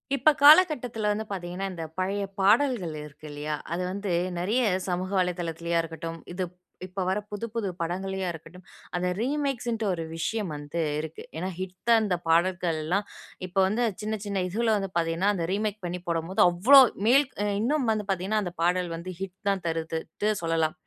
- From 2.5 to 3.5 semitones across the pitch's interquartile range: No, average, 4.1 semitones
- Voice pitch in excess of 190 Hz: No, medium, 185 Hz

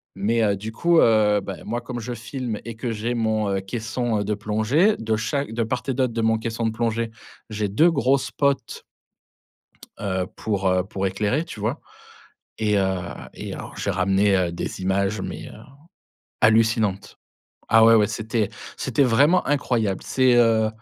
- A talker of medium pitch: No, low, 110 Hz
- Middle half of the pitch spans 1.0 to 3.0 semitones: Yes, average, 2.7 semitones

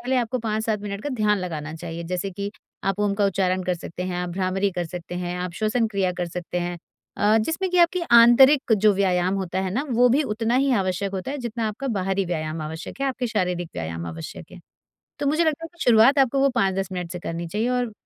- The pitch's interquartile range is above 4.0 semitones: Yes, average, 5.1 semitones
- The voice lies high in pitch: Yes, high, 200 Hz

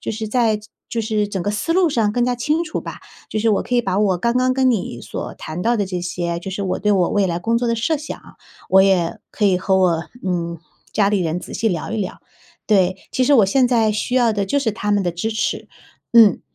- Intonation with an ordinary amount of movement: Yes, average, 4.1 semitones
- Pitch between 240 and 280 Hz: No, high, 210 Hz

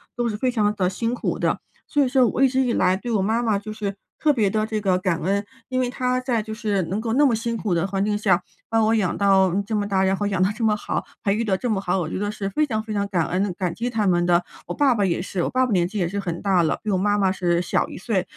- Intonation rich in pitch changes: No, average, 3.3 semitones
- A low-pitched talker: No, high, 205 Hz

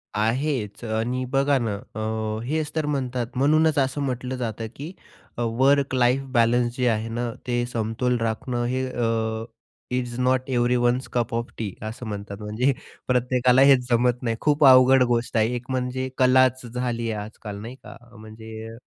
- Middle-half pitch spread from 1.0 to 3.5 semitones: Yes, narrow, 2.4 semitones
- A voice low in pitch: Yes, low, 125 Hz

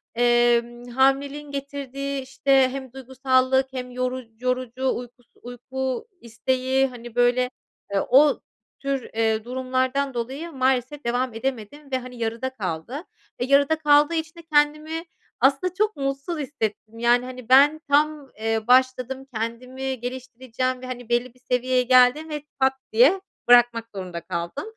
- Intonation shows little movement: Yes, narrow, 2.2 semitones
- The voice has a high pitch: Yes, very high, 255 Hz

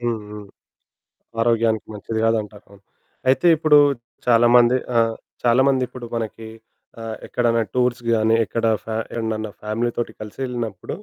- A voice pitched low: Yes, low, 115 Hz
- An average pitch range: No, narrow, 1.5 semitones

